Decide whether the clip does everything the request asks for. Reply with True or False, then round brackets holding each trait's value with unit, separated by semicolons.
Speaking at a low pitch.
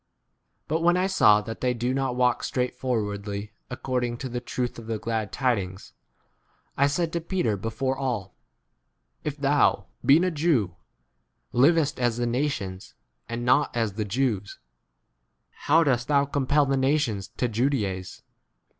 True (125 Hz)